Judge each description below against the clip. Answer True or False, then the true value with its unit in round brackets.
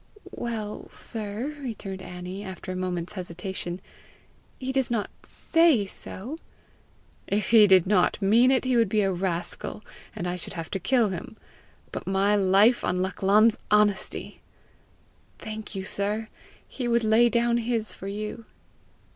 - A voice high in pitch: True (210 Hz)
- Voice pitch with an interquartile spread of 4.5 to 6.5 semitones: False (3.5 semitones)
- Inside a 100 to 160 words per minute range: True (145 wpm)